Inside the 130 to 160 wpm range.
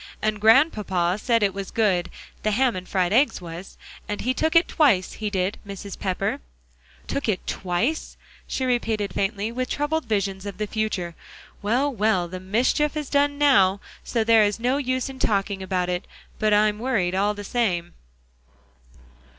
No: average, 170 wpm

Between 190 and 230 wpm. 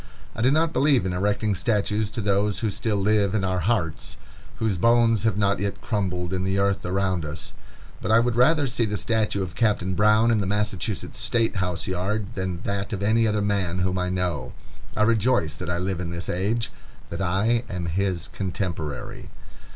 Yes: average, 195 wpm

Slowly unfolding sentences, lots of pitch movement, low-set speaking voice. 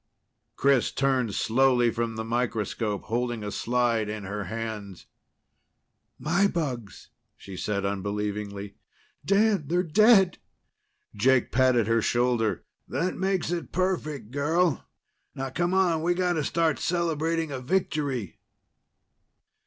Yes: slow, 120 wpm; wide, 7.1 semitones; low, 130 Hz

